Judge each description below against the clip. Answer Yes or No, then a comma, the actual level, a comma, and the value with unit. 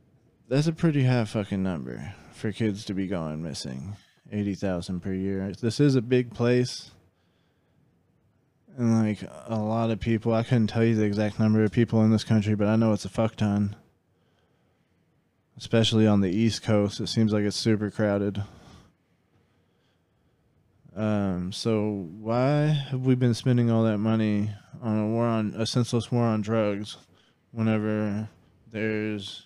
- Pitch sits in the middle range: No, low, 110 Hz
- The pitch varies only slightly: Yes, narrow, 2.1 semitones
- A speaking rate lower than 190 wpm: Yes, average, 160 wpm